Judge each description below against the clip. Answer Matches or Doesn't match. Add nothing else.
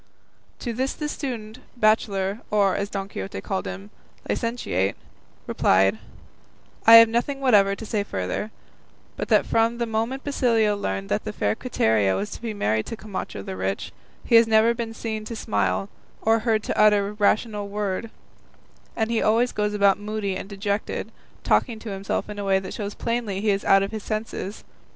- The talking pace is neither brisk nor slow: Matches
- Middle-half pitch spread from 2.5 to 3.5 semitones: Matches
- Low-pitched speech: Doesn't match